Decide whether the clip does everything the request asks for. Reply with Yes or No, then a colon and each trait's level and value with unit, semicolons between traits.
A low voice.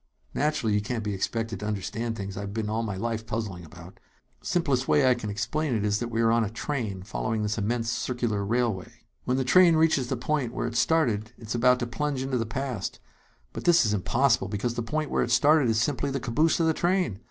Yes: low, 115 Hz